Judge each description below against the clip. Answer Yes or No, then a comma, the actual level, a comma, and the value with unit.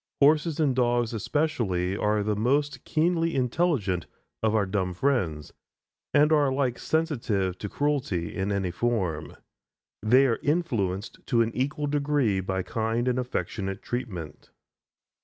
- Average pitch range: No, wide, 6.9 semitones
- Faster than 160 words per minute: No, slow, 135 wpm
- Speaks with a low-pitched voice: Yes, low, 120 Hz